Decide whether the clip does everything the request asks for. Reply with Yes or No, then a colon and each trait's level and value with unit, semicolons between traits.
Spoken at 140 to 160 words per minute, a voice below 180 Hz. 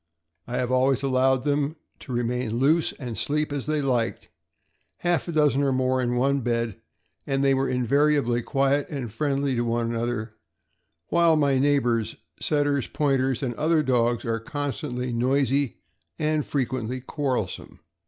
Yes: average, 155 wpm; low, 135 Hz